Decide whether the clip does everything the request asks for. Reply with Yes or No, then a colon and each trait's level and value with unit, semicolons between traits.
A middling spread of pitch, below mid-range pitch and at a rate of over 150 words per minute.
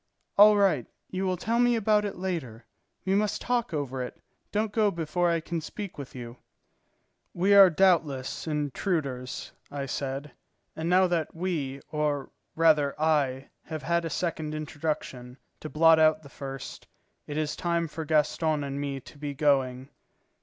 No: average, 4.2 semitones; medium, 155 Hz; average, 160 wpm